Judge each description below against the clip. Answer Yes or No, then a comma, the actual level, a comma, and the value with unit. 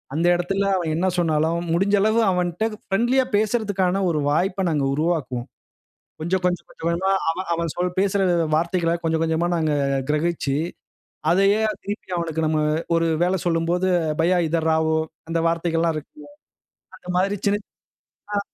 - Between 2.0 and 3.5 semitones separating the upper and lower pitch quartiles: Yes, average, 3.1 semitones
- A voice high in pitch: No, medium, 170 Hz